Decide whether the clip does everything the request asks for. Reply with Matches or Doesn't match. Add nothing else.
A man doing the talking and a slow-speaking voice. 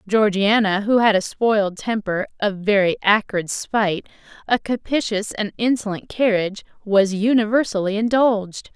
Doesn't match